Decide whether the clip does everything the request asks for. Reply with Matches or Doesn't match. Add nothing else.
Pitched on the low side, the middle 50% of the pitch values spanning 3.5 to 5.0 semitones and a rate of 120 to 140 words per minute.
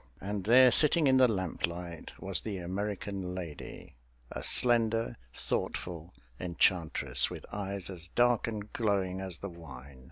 Matches